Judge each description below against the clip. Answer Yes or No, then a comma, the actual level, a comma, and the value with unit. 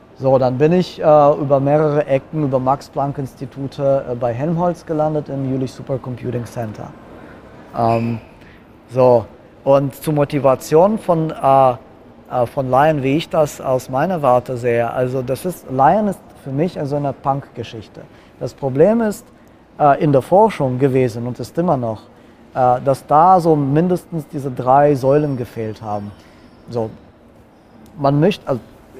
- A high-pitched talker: No, low, 135 Hz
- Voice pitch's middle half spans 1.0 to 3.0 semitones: No, average, 3.4 semitones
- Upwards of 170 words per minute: No, average, 150 wpm